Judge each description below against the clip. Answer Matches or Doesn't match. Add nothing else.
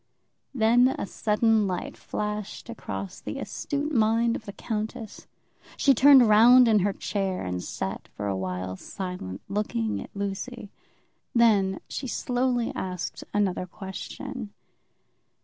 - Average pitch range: Matches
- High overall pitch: Matches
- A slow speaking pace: Matches